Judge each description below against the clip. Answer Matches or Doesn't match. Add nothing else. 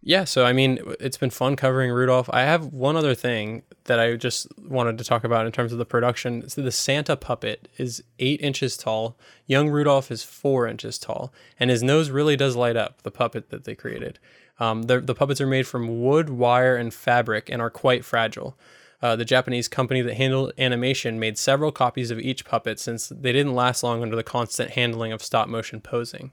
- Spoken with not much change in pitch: Matches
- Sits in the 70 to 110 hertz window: Doesn't match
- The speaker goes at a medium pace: Doesn't match